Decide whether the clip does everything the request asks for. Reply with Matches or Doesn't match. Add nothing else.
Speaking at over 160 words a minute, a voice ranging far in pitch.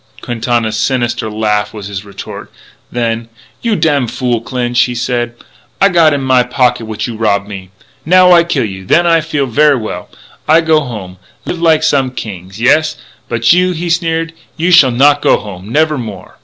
Matches